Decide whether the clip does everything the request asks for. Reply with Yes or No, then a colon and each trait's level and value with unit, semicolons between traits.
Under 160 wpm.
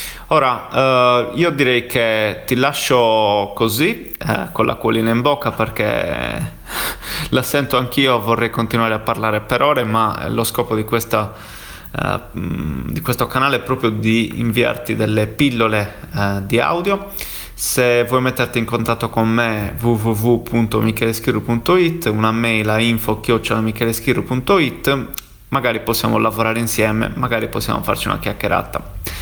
Yes: average, 130 wpm